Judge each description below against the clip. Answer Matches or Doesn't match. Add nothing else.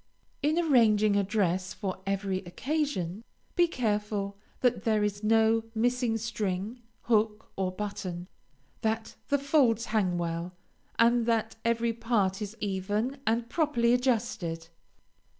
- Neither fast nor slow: Doesn't match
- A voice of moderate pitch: Doesn't match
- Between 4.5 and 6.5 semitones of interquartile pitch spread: Doesn't match